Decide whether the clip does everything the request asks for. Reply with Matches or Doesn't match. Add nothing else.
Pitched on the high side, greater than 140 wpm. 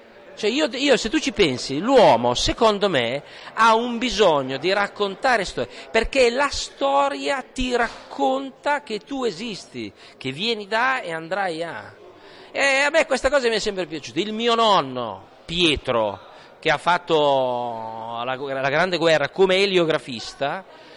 Matches